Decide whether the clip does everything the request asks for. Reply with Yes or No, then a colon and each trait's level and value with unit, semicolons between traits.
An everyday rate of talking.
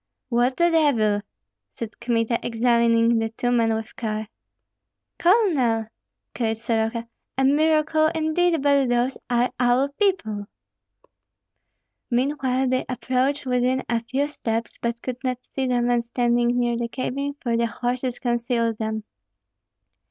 No: slow, 130 wpm